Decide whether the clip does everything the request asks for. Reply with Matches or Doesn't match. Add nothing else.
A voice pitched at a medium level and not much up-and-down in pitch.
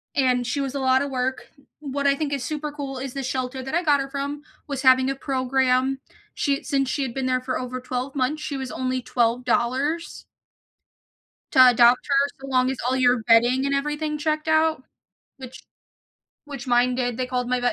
Doesn't match